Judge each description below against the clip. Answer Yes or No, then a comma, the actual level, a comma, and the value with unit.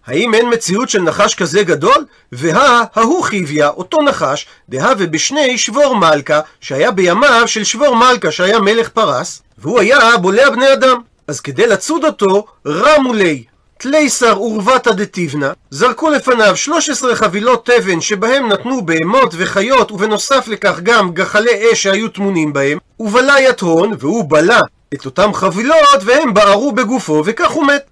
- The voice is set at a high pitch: Yes, high, 225 Hz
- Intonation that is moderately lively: No, wide, 5.7 semitones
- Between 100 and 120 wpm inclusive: No, average, 145 wpm